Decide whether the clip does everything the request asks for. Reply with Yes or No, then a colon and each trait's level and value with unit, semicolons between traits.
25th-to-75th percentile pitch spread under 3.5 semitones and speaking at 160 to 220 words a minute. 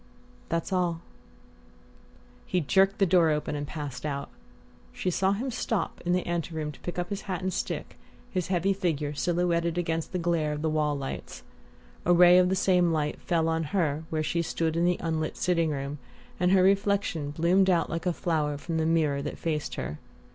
Yes: average, 2.8 semitones; average, 200 wpm